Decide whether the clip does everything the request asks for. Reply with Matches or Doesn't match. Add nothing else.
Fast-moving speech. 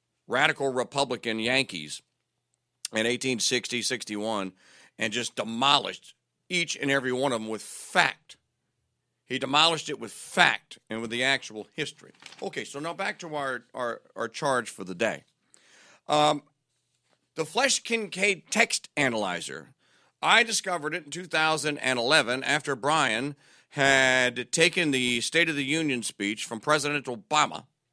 Doesn't match